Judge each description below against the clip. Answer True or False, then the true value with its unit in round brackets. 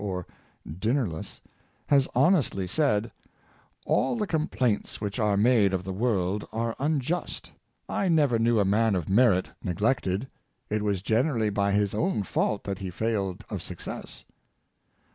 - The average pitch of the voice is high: False (105 Hz)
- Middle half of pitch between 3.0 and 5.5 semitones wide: True (4.5 semitones)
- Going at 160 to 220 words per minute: False (150 wpm)